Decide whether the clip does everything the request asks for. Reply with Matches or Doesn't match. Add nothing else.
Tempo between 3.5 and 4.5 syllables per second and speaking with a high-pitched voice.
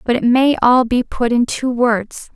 Matches